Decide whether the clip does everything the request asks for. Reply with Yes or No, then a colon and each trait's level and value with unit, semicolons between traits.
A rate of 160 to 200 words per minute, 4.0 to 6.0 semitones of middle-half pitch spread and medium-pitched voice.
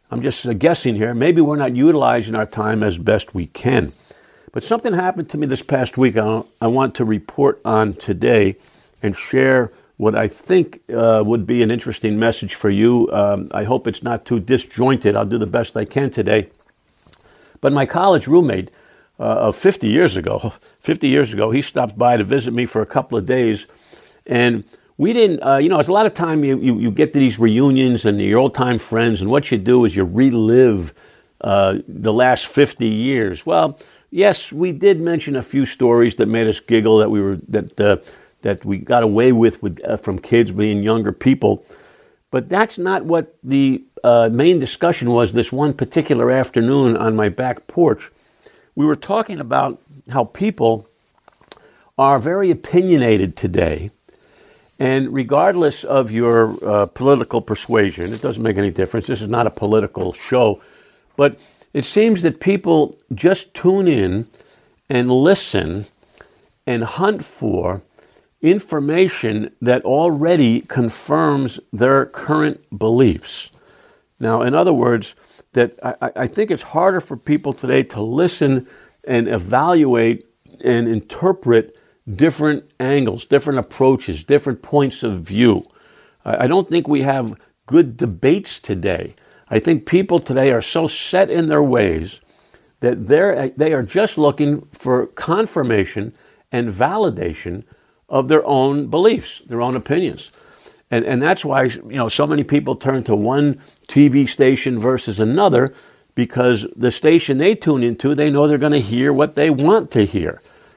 No: average, 165 wpm; average, 4.7 semitones; low, 130 Hz